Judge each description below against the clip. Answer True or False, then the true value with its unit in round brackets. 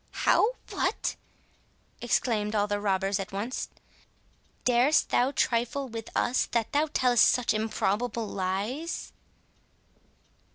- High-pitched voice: True (230 Hz)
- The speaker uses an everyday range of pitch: True (3.5 semitones)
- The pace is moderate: False (110 wpm)